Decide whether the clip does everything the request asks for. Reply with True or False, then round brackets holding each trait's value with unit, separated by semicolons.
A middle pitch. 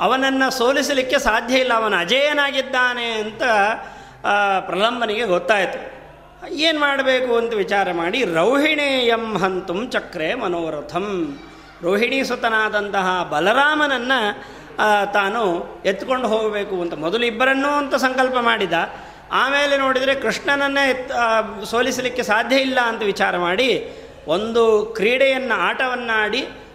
False (235 Hz)